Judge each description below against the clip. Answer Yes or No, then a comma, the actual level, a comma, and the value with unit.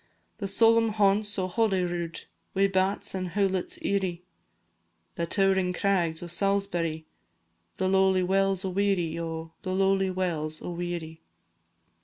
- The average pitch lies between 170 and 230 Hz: Yes, medium, 185 Hz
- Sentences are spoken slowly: Yes, slow, 130 wpm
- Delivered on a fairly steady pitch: Yes, narrow, 2.2 semitones